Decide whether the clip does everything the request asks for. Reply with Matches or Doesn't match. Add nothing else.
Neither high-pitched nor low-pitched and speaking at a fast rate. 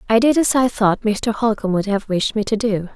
Doesn't match